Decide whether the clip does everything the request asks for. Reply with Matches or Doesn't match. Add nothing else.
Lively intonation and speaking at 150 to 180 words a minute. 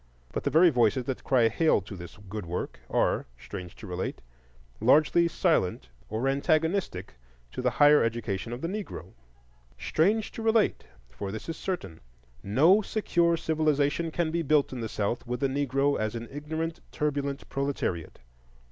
Matches